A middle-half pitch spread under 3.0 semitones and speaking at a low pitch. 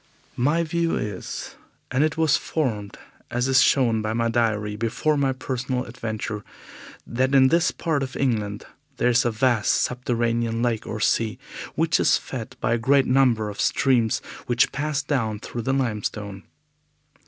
No: average, 3.4 semitones; low, 120 Hz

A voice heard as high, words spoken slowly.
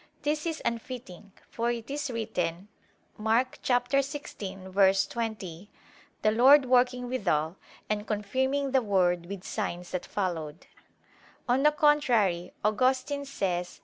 Yes: high, 225 Hz; slow, 115 wpm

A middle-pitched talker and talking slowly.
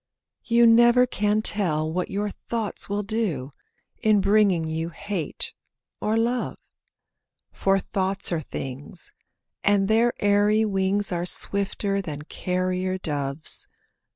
No: high, 195 Hz; slow, 120 wpm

